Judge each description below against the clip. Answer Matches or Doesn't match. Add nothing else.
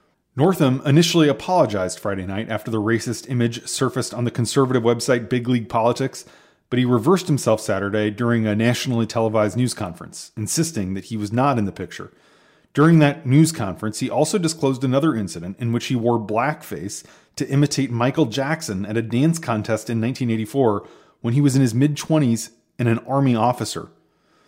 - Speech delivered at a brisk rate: Doesn't match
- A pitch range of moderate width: Matches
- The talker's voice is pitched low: Matches